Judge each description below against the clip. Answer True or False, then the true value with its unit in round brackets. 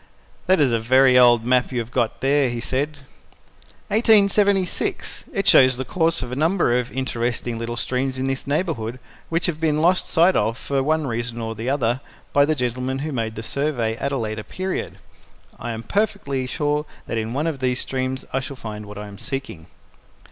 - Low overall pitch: True (130 Hz)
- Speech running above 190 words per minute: True (200 wpm)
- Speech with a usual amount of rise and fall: True (4.2 semitones)